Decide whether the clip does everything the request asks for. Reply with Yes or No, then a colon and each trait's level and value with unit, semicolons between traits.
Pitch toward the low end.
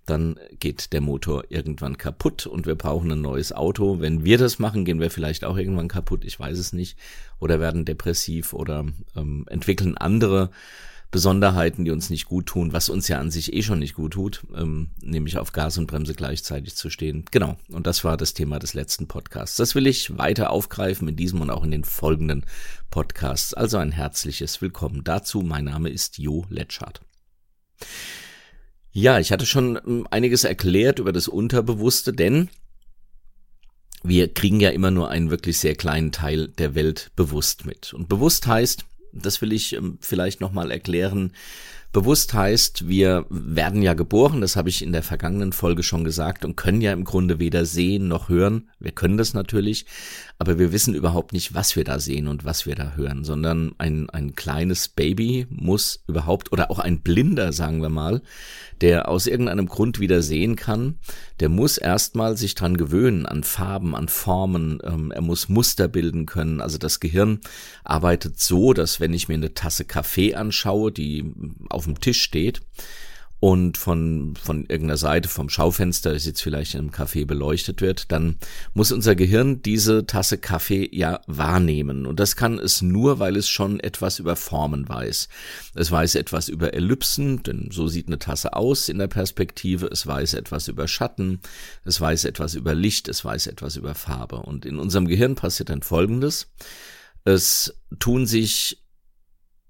Yes: very low, 85 Hz